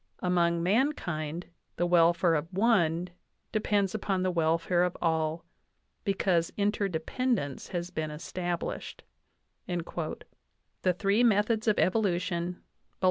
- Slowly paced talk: Yes, slow, 105 wpm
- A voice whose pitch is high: No, medium, 175 Hz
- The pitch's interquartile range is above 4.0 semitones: No, average, 3.0 semitones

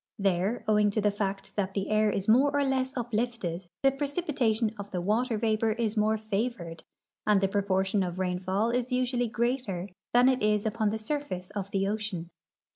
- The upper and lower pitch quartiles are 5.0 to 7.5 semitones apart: No, average, 3.6 semitones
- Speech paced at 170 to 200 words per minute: Yes, average, 185 wpm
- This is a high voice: Yes, high, 215 Hz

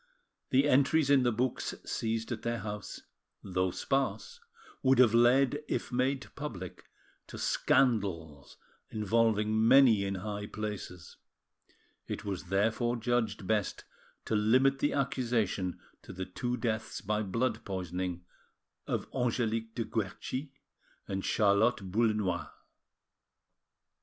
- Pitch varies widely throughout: No, average, 4.2 semitones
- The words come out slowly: Yes, slow, 115 wpm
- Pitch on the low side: Yes, low, 110 Hz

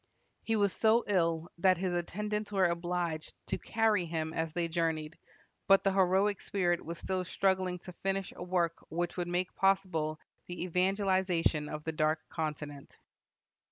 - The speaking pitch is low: No, medium, 180 Hz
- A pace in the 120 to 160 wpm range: Yes, average, 155 wpm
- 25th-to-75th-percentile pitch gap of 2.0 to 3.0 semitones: Yes, average, 2.7 semitones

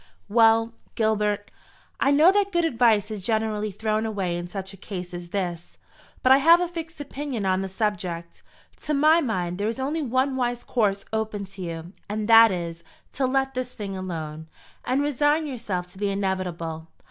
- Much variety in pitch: Yes, wide, 5.7 semitones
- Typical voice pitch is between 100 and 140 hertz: No, high, 215 Hz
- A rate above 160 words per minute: Yes, average, 180 wpm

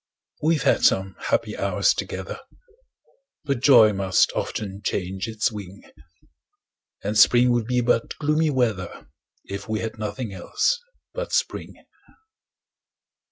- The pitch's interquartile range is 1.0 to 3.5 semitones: No, average, 4.4 semitones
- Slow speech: Yes, slow, 120 wpm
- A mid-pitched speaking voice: No, low, 110 Hz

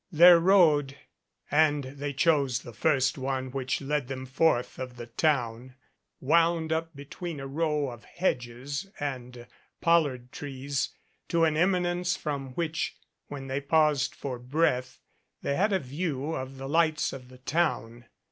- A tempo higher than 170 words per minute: No, average, 150 wpm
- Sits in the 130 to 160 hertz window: Yes, medium, 140 Hz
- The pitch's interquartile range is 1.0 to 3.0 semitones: No, average, 3.8 semitones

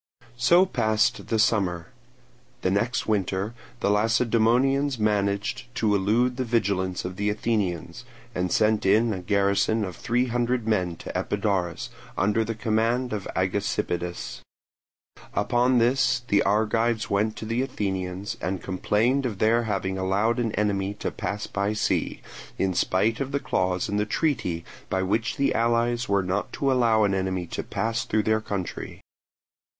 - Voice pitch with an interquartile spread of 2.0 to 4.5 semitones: Yes, average, 3.3 semitones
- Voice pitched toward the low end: Yes, low, 105 Hz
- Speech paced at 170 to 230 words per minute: No, average, 155 wpm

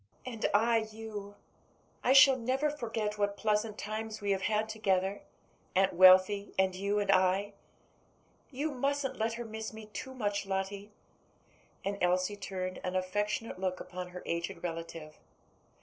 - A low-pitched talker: No, high, 205 Hz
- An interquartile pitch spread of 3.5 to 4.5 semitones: No, average, 2.9 semitones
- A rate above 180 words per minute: No, average, 150 wpm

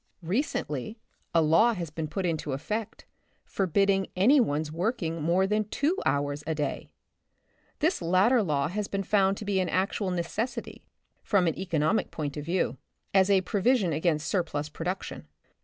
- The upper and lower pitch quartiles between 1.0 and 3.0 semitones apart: No, average, 4.4 semitones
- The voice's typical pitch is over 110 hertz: Yes, medium, 185 Hz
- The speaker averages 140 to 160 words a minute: No, average, 170 wpm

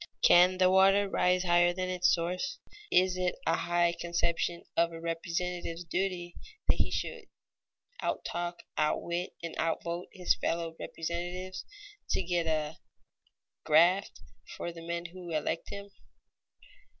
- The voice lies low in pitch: No, medium, 175 Hz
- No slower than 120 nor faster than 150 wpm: Yes, average, 140 wpm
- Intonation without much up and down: Yes, narrow, 1.5 semitones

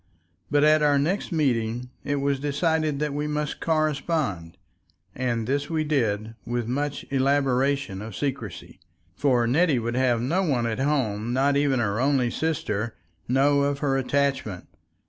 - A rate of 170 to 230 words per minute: No, average, 150 wpm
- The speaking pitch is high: No, low, 135 Hz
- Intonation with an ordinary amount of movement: Yes, average, 3.6 semitones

